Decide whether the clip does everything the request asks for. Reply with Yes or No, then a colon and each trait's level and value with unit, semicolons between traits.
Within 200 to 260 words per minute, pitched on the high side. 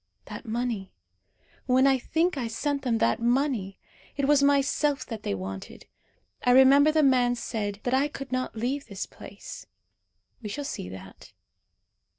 No: average, 160 wpm; very high, 255 Hz